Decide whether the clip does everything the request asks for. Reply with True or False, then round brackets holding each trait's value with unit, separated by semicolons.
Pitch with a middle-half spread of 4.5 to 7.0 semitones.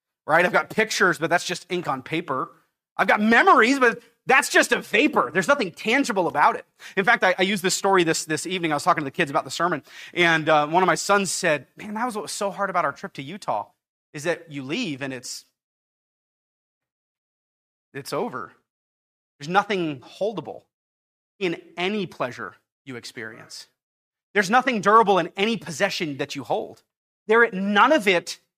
True (5.2 semitones)